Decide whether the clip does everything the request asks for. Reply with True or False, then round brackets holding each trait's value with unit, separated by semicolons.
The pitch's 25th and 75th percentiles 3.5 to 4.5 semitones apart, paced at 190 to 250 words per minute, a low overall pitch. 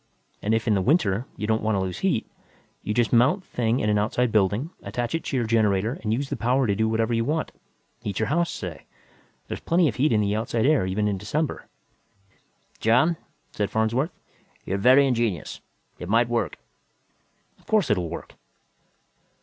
True (3.8 semitones; 195 wpm; 115 Hz)